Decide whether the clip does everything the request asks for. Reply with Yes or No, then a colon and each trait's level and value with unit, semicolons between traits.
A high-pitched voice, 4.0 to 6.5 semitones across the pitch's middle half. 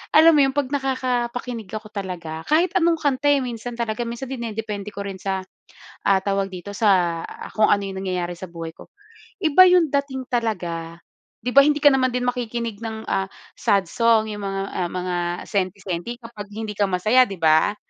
Yes: high, 215 Hz; average, 4.7 semitones